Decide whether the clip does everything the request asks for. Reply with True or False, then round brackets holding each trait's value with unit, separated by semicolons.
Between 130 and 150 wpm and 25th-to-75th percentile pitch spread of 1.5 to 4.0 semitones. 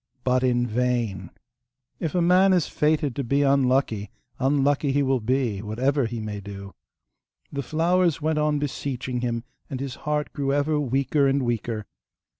False (160 wpm; 3.5 semitones)